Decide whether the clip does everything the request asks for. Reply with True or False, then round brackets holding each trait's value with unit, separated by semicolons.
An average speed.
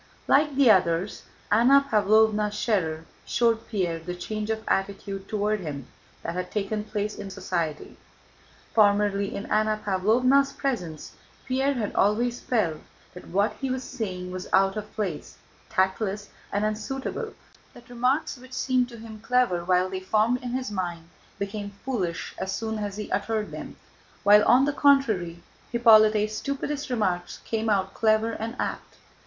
True (150 wpm)